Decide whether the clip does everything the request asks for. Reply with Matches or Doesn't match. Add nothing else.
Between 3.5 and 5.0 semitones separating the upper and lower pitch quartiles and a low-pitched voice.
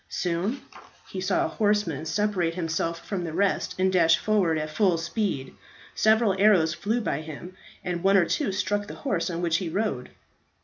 Doesn't match